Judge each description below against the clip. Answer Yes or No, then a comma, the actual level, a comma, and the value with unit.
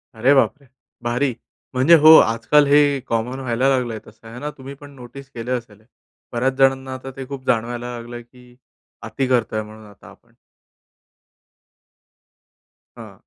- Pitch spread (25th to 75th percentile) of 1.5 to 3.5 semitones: Yes, narrow, 2.5 semitones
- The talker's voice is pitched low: Yes, low, 125 Hz